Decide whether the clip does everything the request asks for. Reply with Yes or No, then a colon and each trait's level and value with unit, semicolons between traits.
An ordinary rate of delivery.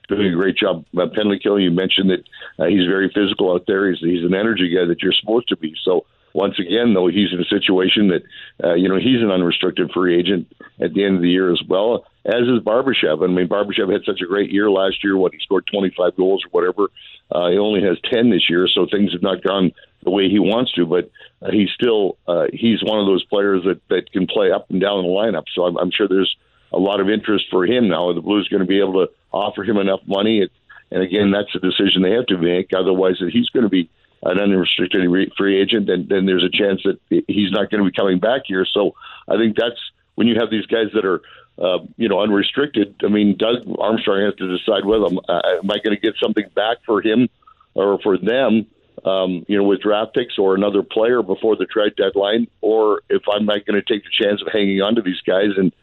No: fast, 250 wpm